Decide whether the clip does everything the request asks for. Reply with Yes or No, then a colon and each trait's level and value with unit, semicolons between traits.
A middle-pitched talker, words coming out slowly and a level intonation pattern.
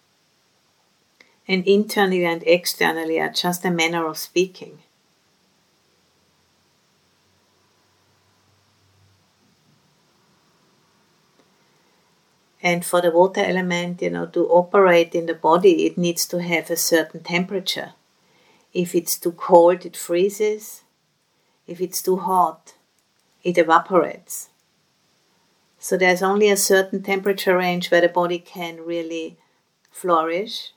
Yes: medium, 175 Hz; slow, 105 wpm; narrow, 1.9 semitones